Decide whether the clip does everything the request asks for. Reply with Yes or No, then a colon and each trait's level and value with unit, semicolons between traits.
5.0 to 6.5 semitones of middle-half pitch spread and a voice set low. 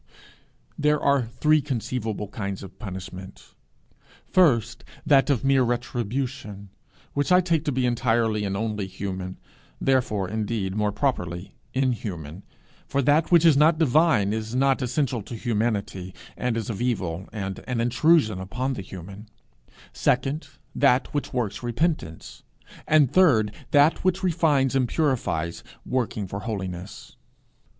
Yes: wide, 5.6 semitones; low, 120 Hz